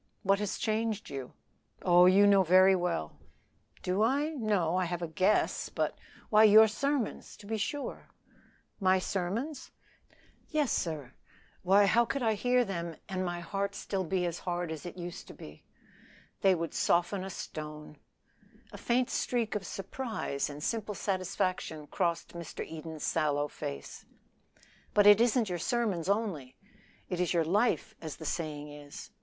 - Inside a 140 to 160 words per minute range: Yes, average, 155 wpm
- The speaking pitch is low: No, medium, 185 Hz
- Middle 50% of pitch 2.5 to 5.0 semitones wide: Yes, average, 4.4 semitones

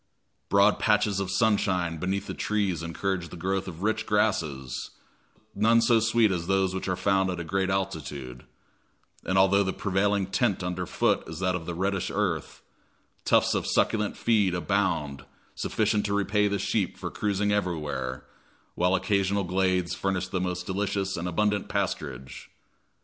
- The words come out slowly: No, average, 160 wpm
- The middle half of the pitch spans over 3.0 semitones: No, narrow, 2.4 semitones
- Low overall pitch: Yes, very low, 95 Hz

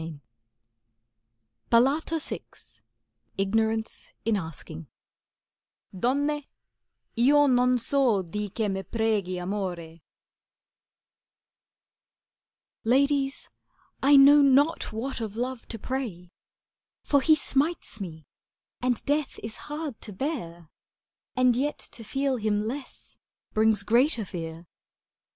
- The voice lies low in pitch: No, high, 235 Hz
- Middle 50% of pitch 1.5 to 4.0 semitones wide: No, wide, 5.5 semitones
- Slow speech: Yes, slow, 100 wpm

